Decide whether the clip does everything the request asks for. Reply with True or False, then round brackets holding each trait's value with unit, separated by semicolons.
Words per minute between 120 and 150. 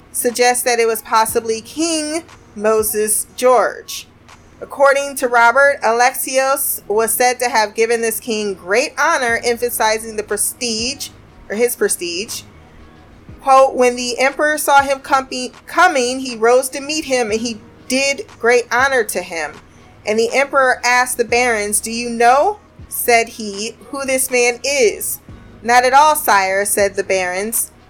True (145 wpm)